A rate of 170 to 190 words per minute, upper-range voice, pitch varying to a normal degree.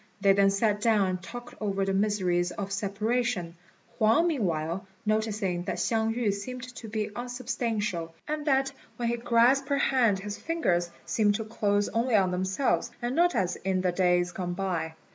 Yes: average, 175 wpm; high, 210 Hz; average, 4.1 semitones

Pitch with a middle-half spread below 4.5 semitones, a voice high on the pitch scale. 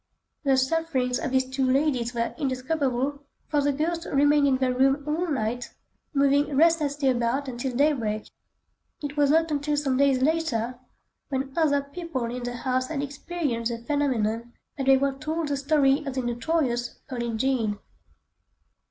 Yes: average, 2.8 semitones; very high, 270 Hz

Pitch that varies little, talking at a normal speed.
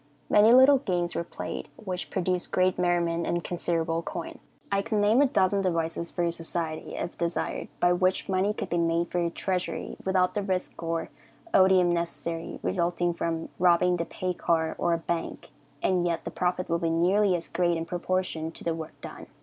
Yes: narrow, 1.8 semitones; average, 190 wpm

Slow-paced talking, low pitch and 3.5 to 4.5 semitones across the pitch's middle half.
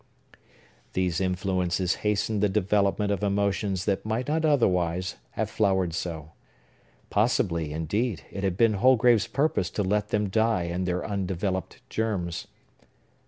No: slow, 130 wpm; low, 100 Hz; average, 2.8 semitones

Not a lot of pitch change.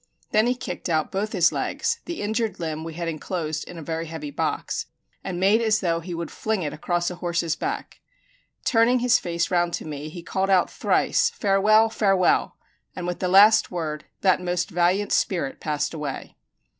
No: average, 4.0 semitones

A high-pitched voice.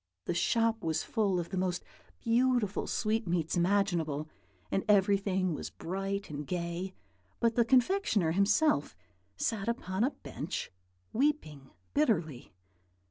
Yes: high, 195 Hz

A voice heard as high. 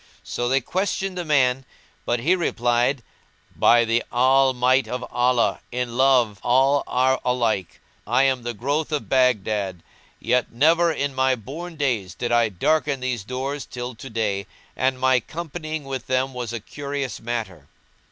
No: low, 130 Hz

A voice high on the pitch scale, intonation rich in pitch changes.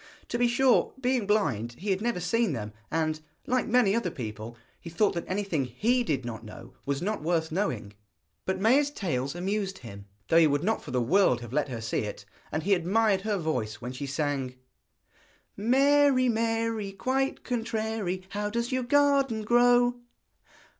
Yes: high, 195 Hz; wide, 8.7 semitones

